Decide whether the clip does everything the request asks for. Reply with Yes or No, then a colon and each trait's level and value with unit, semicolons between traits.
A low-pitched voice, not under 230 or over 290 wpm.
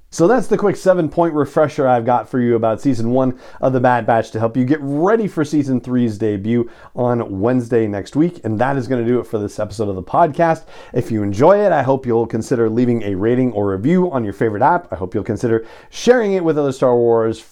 Yes: low, 125 Hz; fast, 245 wpm